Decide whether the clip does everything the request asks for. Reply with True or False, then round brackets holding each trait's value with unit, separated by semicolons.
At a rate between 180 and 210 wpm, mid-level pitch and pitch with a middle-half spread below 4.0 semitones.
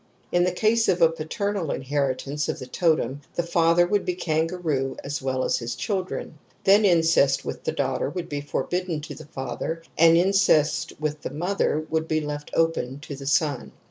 True (185 wpm; 160 Hz; 3.5 semitones)